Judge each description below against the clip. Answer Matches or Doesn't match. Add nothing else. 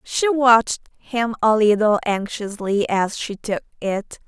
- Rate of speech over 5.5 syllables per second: Doesn't match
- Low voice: Doesn't match